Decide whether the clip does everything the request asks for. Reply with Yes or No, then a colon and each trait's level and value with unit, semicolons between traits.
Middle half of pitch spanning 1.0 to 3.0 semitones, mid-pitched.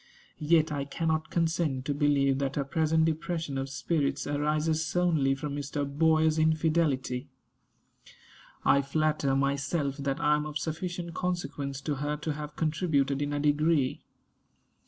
Yes: narrow, 2.4 semitones; medium, 150 Hz